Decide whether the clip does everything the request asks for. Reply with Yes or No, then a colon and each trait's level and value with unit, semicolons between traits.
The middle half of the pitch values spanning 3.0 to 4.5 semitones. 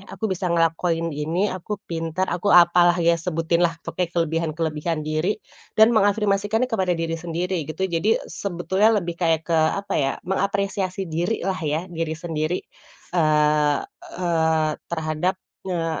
No: narrow, 2.6 semitones